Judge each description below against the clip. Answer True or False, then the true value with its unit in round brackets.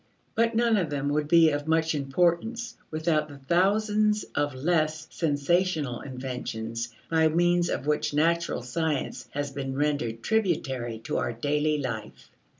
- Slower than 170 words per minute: True (145 wpm)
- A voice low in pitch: False (150 Hz)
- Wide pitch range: False (4.0 semitones)